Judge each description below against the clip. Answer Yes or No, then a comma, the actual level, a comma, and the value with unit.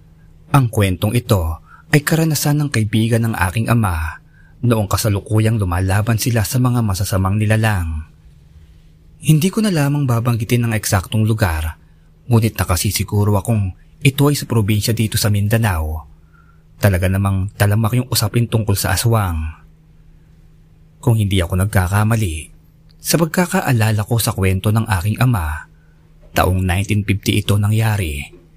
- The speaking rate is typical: Yes, average, 125 wpm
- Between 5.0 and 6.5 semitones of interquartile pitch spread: No, average, 3.8 semitones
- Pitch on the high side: No, low, 105 Hz